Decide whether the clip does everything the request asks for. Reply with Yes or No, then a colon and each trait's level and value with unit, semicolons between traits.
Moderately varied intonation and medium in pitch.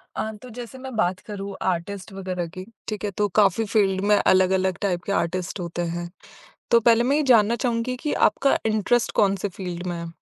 No: average, 3.8 semitones; high, 200 Hz